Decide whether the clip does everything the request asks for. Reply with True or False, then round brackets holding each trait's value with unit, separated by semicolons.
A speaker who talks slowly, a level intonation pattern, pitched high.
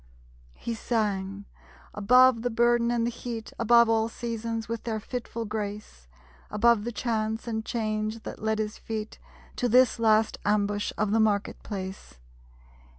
False (150 wpm; 1.8 semitones; 220 Hz)